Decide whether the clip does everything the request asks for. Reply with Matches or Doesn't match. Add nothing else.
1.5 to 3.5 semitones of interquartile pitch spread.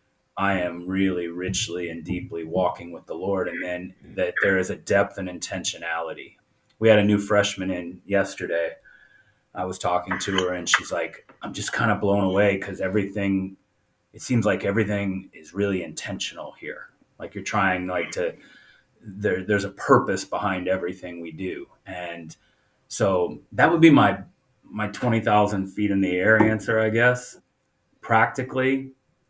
Matches